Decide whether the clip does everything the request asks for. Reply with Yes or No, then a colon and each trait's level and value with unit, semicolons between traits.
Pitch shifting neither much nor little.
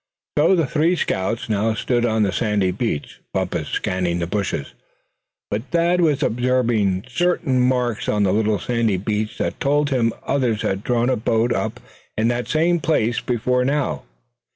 Yes: average, 4.1 semitones